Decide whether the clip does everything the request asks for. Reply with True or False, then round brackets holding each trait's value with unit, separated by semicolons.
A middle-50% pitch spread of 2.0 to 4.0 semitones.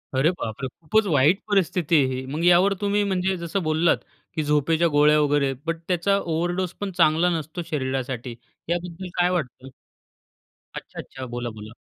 False (4.6 semitones)